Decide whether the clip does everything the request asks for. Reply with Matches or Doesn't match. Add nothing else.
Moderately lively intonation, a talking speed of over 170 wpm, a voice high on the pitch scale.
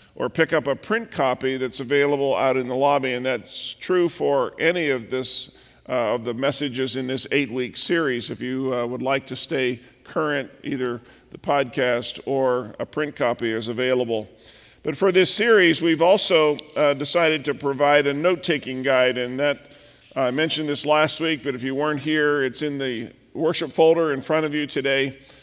Doesn't match